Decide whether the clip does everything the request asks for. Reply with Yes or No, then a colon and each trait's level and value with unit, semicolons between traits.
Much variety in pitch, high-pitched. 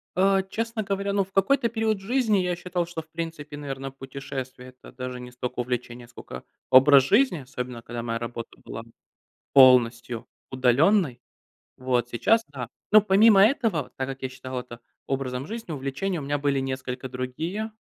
No: wide, 7.3 semitones; low, 135 Hz